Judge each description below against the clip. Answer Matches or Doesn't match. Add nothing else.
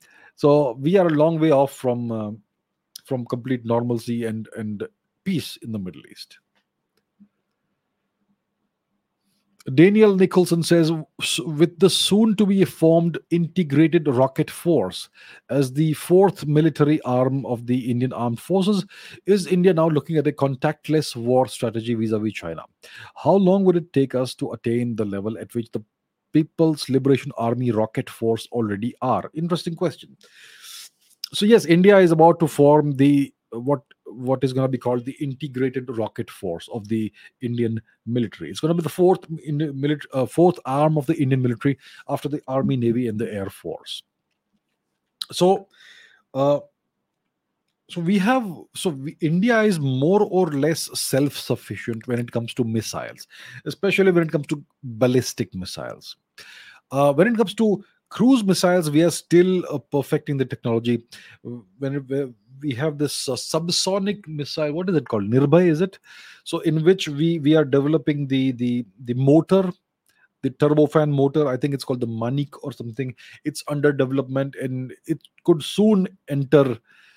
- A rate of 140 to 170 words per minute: Matches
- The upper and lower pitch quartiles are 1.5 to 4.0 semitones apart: Doesn't match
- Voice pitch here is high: Doesn't match